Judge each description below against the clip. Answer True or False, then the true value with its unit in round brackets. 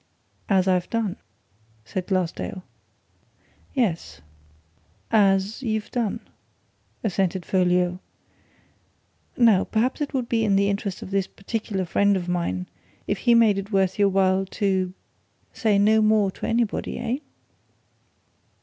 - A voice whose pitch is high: True (200 Hz)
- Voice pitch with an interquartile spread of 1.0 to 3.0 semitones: True (2.7 semitones)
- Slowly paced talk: True (120 wpm)